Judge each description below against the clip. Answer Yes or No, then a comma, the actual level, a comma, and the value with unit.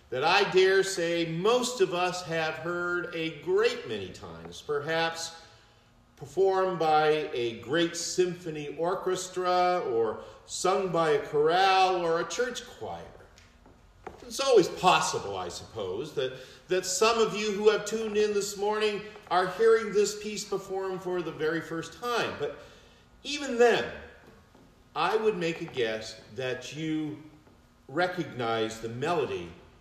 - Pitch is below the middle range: No, medium, 180 Hz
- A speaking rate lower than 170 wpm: Yes, slow, 135 wpm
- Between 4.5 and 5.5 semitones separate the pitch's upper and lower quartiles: Yes, average, 4.8 semitones